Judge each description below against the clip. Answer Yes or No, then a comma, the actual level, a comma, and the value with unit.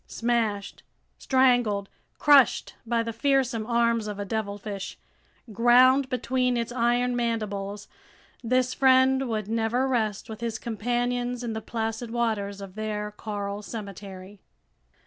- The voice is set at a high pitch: Yes, high, 230 Hz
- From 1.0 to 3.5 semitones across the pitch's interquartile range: Yes, average, 2.8 semitones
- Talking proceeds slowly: Yes, slow, 125 wpm